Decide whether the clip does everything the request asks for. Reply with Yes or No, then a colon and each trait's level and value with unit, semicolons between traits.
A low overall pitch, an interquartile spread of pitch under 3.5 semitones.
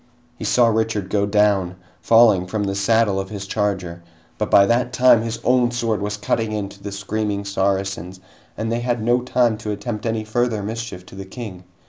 Yes: low, 105 Hz; average, 2.7 semitones